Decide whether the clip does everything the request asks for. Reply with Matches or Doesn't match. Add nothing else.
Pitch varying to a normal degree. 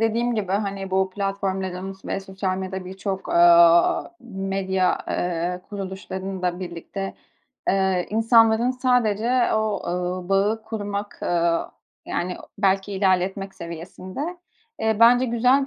Matches